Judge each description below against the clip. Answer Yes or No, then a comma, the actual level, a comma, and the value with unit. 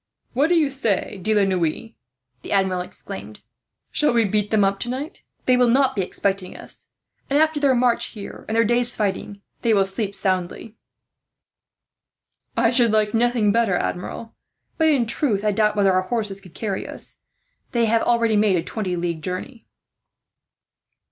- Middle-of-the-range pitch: No, high, 215 Hz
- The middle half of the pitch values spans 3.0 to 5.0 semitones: Yes, average, 3.7 semitones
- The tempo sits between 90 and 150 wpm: No, average, 170 wpm